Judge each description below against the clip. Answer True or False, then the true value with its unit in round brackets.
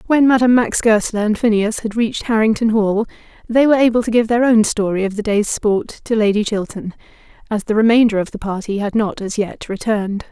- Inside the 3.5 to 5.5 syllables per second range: False (5.8 syllables/s)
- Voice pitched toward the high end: True (220 Hz)